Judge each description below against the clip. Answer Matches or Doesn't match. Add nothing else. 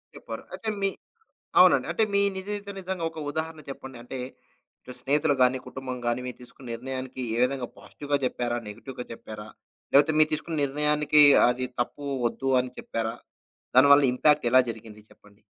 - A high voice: Doesn't match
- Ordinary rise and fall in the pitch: Matches